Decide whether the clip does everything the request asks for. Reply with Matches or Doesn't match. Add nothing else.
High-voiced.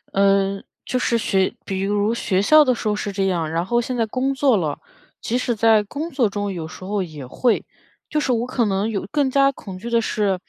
Matches